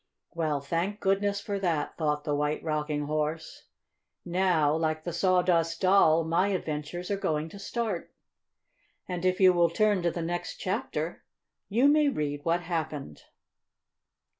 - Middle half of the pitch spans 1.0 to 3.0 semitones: No, average, 3.8 semitones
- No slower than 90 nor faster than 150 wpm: Yes, average, 145 wpm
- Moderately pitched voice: Yes, medium, 170 Hz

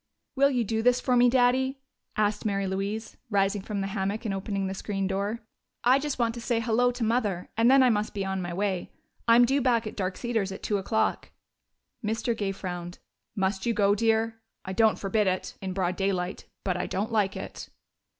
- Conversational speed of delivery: No, fast, 210 wpm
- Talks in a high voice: Yes, high, 210 Hz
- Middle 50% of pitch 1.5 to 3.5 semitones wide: Yes, average, 3.2 semitones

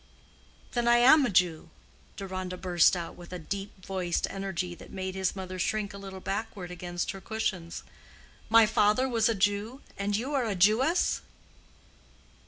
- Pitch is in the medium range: No, high, 195 Hz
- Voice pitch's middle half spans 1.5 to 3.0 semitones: No, average, 3.4 semitones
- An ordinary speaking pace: Yes, average, 165 wpm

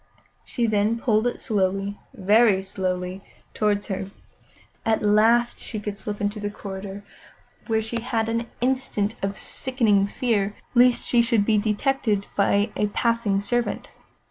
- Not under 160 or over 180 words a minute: No, average, 145 wpm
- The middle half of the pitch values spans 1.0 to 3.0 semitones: Yes, narrow, 2.6 semitones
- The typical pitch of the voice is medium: No, high, 210 Hz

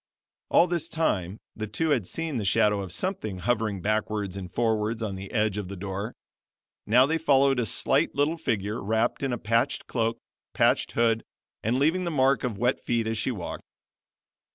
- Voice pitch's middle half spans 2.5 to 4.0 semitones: No, average, 4.5 semitones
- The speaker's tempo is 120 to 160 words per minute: No, average, 185 wpm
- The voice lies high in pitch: No, low, 115 Hz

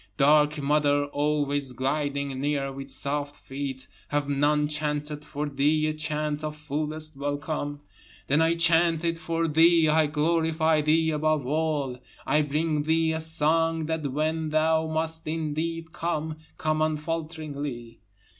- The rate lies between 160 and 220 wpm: No, slow, 135 wpm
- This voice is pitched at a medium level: Yes, medium, 150 Hz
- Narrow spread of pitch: Yes, narrow, 1.8 semitones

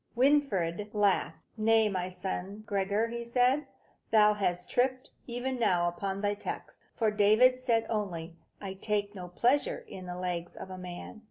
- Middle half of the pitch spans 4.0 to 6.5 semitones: Yes, average, 4.3 semitones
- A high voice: Yes, high, 210 Hz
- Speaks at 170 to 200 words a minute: No, average, 160 wpm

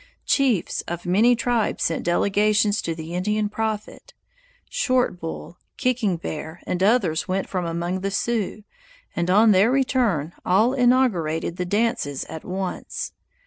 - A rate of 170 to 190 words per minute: No, average, 140 wpm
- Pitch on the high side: Yes, high, 195 Hz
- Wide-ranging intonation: No, average, 5.0 semitones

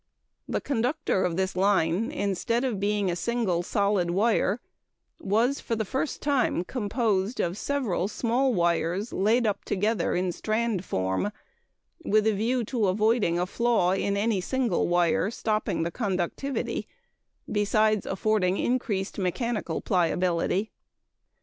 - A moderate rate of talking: No, slow, 130 wpm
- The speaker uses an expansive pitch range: No, average, 4.1 semitones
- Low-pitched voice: No, high, 205 Hz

